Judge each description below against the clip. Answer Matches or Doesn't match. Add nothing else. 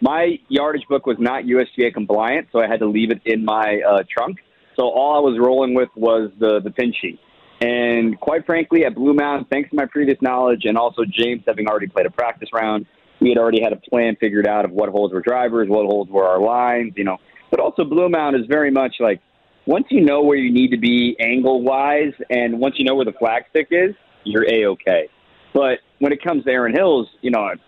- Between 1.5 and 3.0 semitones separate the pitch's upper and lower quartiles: Doesn't match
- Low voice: Matches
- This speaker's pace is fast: Matches